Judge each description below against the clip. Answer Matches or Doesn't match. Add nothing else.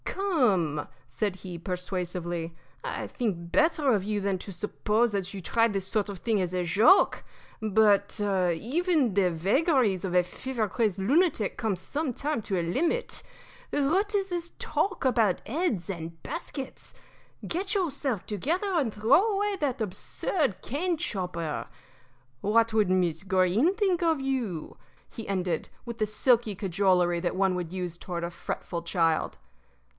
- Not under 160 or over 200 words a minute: Doesn't match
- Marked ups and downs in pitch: Matches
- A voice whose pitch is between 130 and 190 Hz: Doesn't match